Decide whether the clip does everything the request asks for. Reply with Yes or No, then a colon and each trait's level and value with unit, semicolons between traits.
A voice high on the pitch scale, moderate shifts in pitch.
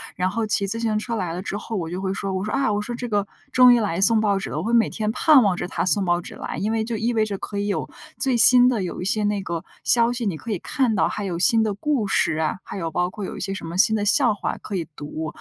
Yes: high, 210 Hz; average, 3.3 semitones